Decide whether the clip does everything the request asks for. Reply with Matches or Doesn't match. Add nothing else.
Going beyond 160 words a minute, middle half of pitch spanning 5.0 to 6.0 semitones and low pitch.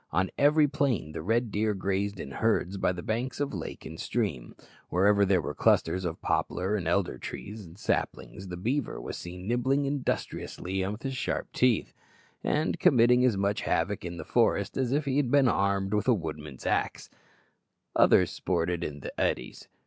Matches